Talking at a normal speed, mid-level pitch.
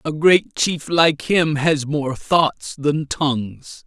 Yes: average, 155 wpm; medium, 150 Hz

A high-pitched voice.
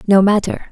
Yes: high, 200 Hz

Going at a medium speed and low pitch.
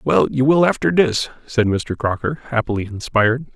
Yes: average, 170 wpm; low, 125 Hz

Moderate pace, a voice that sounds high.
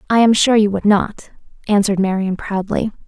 Yes: average, 175 wpm; high, 205 Hz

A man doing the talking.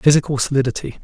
Yes: male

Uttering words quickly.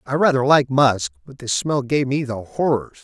Yes: fast, 215 wpm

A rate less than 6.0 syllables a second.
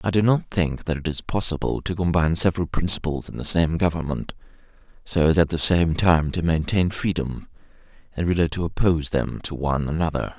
Yes: 5.7 syllables/s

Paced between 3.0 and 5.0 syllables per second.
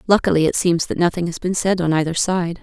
No: 6.1 syllables/s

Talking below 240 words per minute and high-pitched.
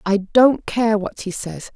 Yes: fast, 205 wpm; high, 210 Hz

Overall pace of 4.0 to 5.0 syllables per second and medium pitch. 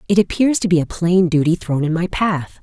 No: 5.3 syllables/s; medium, 175 Hz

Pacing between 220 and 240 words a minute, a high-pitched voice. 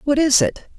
Yes: fast, 230 wpm; very high, 265 Hz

